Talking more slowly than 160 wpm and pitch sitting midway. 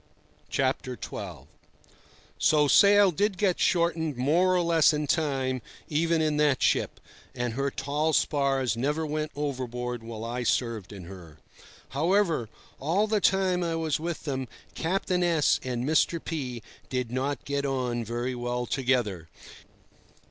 Yes: average, 140 wpm; medium, 145 Hz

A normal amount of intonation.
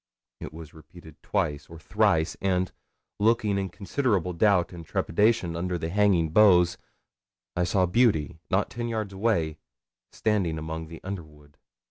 Yes: average, 4.1 semitones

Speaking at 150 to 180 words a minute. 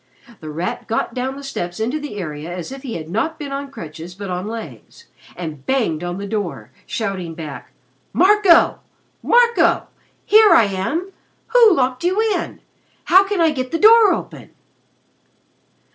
Yes: average, 160 wpm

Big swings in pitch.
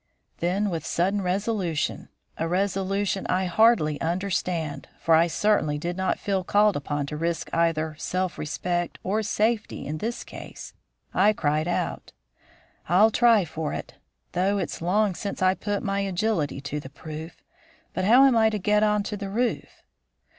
No: average, 4.0 semitones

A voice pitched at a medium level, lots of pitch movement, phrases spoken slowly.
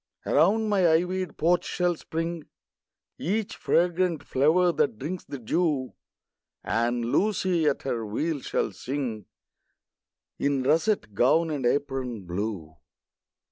Yes: medium, 150 Hz; wide, 6.0 semitones; slow, 115 wpm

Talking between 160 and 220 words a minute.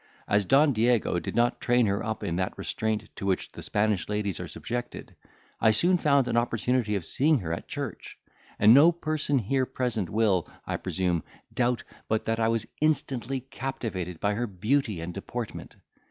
Yes: average, 180 wpm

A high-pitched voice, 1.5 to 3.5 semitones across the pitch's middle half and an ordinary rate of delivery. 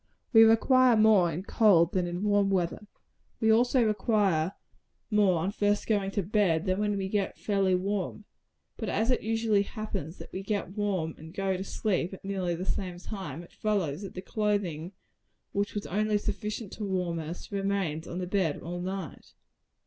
Yes: high, 195 Hz; average, 2.8 semitones; average, 180 wpm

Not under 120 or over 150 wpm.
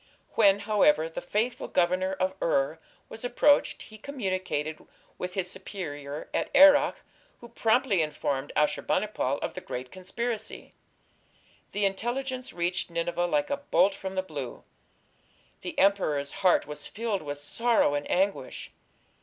Yes: average, 140 wpm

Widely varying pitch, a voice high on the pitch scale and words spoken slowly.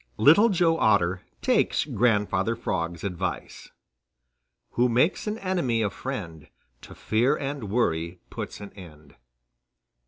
No: wide, 7.3 semitones; low, 110 Hz; slow, 130 wpm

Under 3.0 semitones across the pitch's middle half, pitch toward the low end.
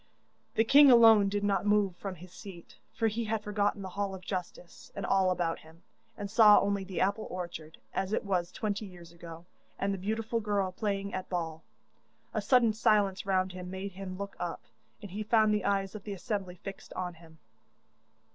No: narrow, 2.4 semitones; high, 195 Hz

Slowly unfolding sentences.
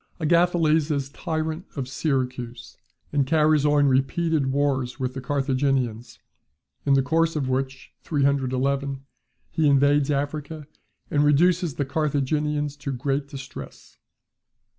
Yes: slow, 120 wpm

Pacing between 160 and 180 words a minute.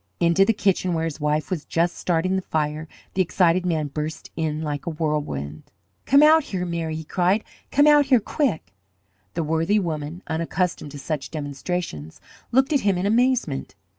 Yes: average, 170 wpm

